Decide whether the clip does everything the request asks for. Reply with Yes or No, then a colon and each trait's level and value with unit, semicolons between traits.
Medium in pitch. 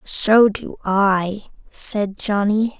No: high, 205 Hz